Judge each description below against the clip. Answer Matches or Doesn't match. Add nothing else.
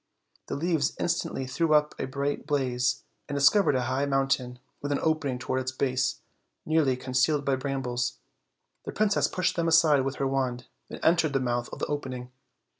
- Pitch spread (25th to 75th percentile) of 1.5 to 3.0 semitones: Matches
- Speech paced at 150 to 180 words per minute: Doesn't match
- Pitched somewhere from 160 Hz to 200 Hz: Doesn't match